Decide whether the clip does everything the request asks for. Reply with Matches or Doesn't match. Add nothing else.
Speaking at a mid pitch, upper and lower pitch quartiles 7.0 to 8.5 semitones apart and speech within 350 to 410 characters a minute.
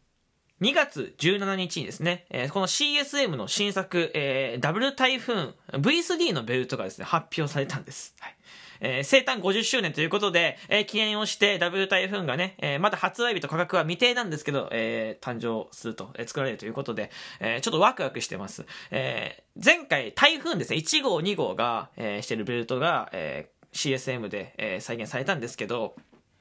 Matches